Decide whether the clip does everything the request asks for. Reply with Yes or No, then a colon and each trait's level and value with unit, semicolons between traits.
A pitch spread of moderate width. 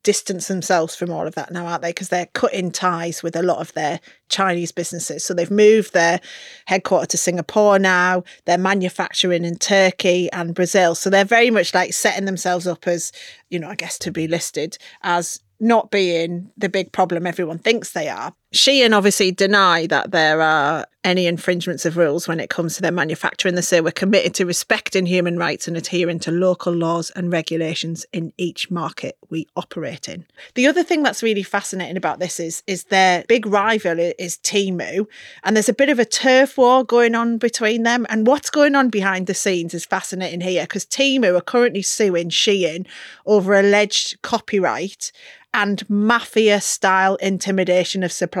Yes: average, 3.1 semitones